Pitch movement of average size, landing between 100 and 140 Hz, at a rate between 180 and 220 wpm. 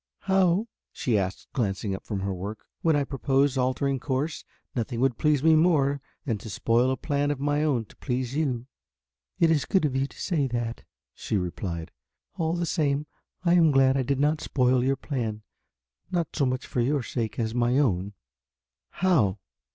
Yes: average, 4.3 semitones; low, 135 Hz; average, 190 wpm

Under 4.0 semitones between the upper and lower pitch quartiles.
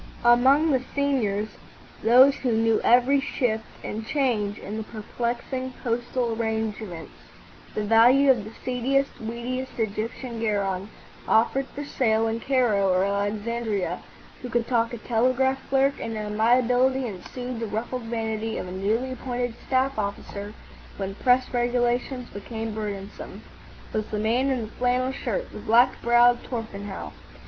Yes: average, 2.9 semitones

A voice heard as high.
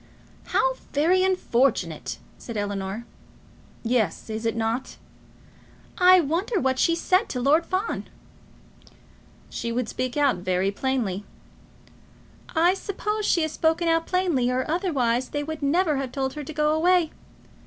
Yes: very high, 285 Hz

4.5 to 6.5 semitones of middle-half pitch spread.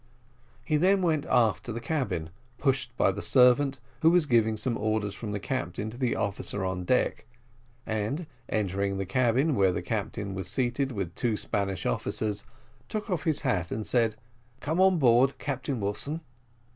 Yes: average, 5.3 semitones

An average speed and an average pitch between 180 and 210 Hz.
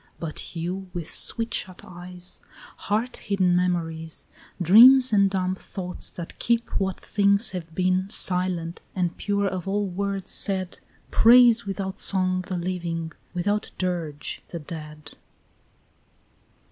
No: slow, 125 wpm; medium, 185 Hz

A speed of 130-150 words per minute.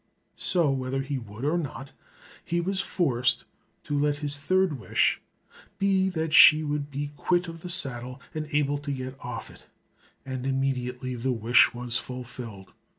No: average, 160 wpm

